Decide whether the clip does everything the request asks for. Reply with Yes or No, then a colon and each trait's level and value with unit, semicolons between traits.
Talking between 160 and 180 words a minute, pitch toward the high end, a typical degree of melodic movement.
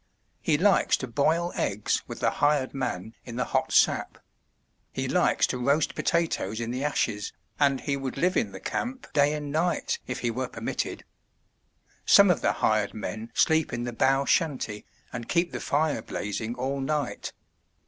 No: average, 175 wpm; low, 135 Hz; average, 4.4 semitones